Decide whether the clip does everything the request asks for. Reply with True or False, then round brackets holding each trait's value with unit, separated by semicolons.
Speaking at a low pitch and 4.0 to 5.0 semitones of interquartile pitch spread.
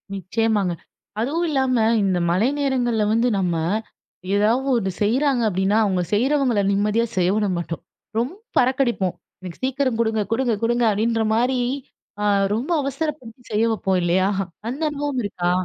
False (230 Hz; 4.5 semitones)